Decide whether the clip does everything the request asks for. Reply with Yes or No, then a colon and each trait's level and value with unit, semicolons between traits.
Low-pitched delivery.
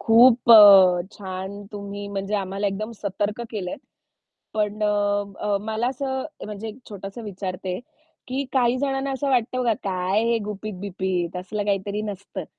No: high, 205 Hz